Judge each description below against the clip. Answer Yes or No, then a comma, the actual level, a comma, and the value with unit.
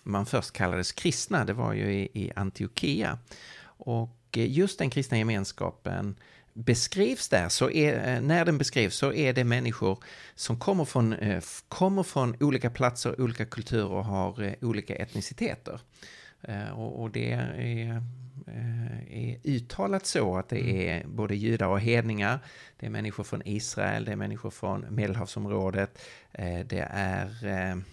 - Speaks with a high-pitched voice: No, low, 115 Hz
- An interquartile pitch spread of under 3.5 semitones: No, average, 3.8 semitones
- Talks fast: No, average, 135 wpm